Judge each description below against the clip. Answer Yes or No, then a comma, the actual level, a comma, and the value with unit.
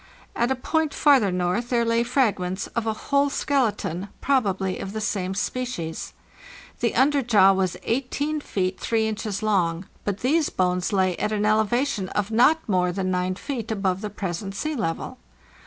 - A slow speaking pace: No, average, 165 wpm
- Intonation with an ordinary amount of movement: Yes, average, 5.0 semitones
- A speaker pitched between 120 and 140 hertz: No, high, 215 Hz